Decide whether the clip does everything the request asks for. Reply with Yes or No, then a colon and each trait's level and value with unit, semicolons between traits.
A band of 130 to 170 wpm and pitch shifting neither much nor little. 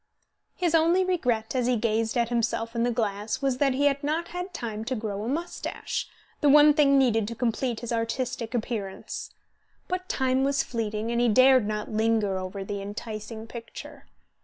No: average, 185 wpm; average, 3.8 semitones